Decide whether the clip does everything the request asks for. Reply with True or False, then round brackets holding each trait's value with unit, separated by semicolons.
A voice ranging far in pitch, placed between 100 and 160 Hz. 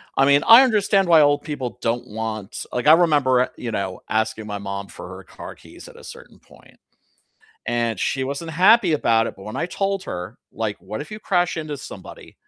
True (7.3 semitones; 135 Hz)